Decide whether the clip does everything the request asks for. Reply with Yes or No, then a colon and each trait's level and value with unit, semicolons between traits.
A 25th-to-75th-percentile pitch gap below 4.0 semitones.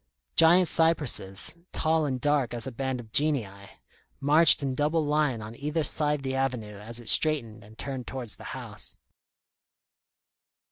No: average, 4.5 semitones